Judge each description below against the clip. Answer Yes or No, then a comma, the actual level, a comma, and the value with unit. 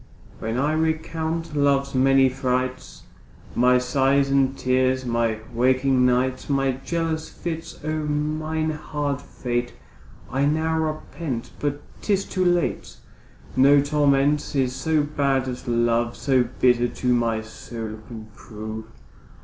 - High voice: No, low, 135 Hz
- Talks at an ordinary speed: No, slow, 125 wpm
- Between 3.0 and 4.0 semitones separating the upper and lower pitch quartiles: Yes, average, 3.4 semitones